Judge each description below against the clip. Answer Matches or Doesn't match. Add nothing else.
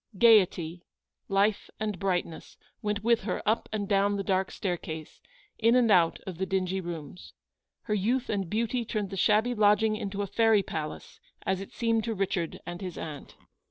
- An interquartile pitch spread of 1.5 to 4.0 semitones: Matches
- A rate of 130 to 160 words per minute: Doesn't match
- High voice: Matches